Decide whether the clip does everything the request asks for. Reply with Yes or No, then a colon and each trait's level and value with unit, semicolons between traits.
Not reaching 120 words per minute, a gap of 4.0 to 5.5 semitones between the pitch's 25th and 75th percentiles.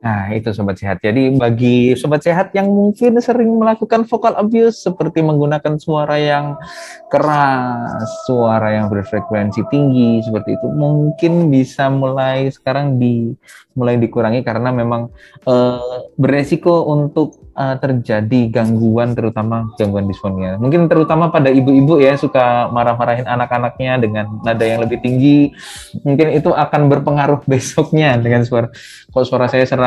No: average, 135 wpm; average, 4.3 semitones